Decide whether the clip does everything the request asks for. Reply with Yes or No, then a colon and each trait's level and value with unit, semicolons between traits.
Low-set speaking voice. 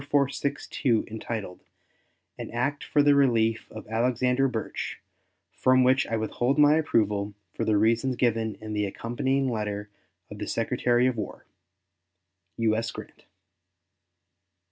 Yes: low, 115 Hz